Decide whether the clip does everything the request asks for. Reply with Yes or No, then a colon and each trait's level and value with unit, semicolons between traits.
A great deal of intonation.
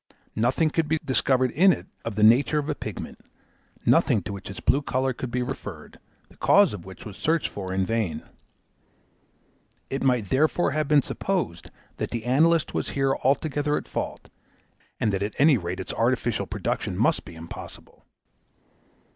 Yes: wide, 6.2 semitones